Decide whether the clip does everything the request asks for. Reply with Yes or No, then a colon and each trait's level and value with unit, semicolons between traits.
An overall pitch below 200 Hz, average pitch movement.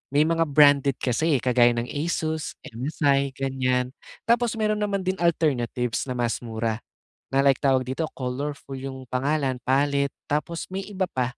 Yes: medium, 140 Hz; average, 3.9 semitones